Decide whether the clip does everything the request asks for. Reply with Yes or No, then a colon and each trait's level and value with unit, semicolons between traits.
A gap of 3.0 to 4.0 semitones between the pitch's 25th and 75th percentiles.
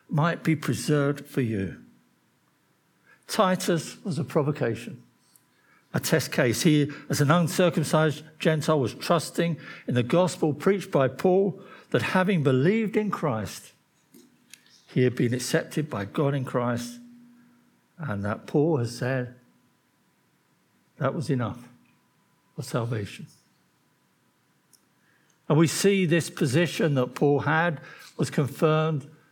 No: average, 4.5 semitones